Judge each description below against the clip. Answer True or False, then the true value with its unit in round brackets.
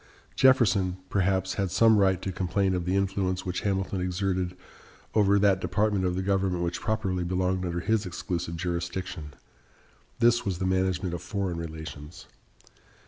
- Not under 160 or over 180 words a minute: False (150 wpm)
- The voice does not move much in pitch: True (1.7 semitones)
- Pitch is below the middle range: True (95 Hz)